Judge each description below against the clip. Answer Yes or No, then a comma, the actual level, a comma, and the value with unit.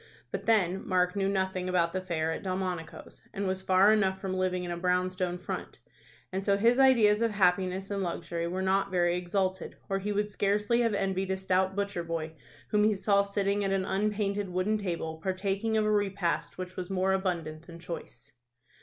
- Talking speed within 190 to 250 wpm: Yes, average, 200 wpm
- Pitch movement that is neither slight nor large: No, narrow, 1.8 semitones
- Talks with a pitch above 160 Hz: Yes, high, 190 Hz